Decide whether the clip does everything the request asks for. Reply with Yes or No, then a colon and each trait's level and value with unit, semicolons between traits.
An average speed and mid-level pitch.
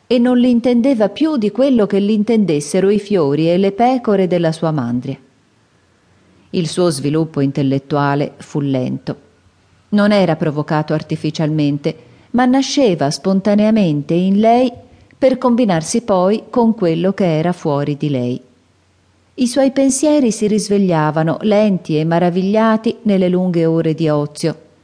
Yes: average, 135 wpm; medium, 175 Hz